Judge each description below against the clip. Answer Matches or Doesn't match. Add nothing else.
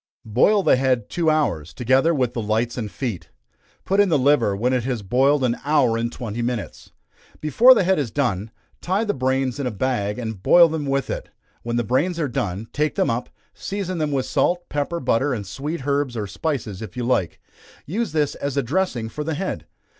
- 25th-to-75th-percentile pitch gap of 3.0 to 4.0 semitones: Doesn't match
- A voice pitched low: Matches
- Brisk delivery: Matches